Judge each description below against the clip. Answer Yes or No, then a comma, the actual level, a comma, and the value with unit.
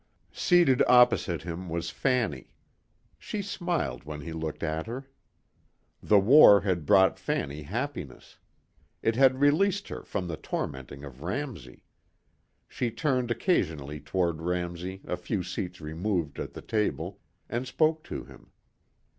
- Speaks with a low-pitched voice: Yes, very low, 95 Hz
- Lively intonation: Yes, wide, 7.9 semitones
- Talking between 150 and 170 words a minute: No, slow, 135 wpm